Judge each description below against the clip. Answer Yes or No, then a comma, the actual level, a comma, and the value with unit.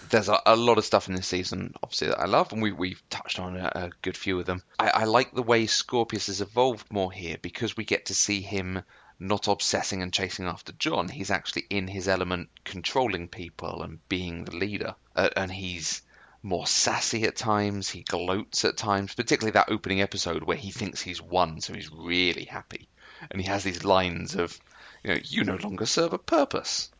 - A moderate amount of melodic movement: No, narrow, 2.1 semitones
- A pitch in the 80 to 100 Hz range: Yes, very low, 95 Hz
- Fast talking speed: Yes, fast, 210 wpm